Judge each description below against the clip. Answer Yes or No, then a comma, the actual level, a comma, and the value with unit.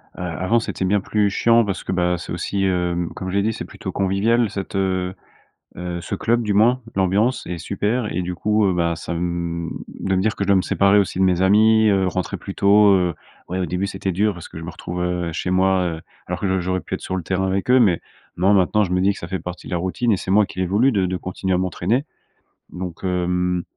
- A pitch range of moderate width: No, narrow, 2.2 semitones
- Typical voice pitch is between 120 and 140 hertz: No, very low, 95 Hz